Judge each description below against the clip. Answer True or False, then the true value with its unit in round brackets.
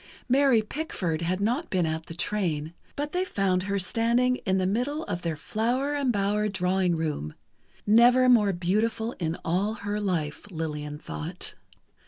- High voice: True (200 Hz)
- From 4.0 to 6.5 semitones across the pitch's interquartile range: True (5.6 semitones)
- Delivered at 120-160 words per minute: True (150 wpm)